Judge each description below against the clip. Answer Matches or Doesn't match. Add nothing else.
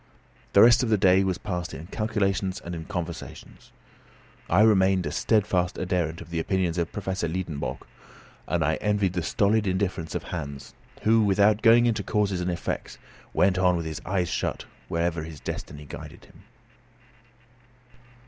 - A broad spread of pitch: Doesn't match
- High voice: Doesn't match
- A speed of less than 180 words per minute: Matches